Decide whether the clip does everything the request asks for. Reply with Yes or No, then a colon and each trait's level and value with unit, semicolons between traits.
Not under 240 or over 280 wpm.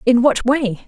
No: fast, 205 wpm